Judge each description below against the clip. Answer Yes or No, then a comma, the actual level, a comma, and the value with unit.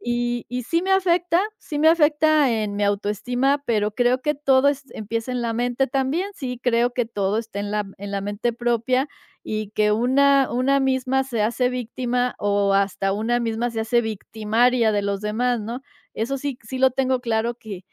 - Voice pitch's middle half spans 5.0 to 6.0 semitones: No, average, 3.5 semitones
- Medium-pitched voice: No, high, 240 Hz